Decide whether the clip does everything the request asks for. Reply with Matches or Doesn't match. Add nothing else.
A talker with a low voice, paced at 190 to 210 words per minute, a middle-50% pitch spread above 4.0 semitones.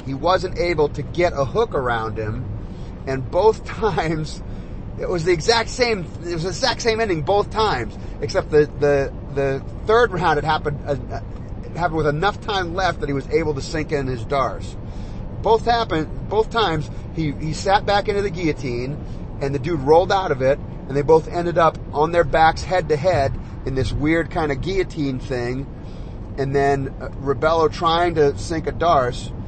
Doesn't match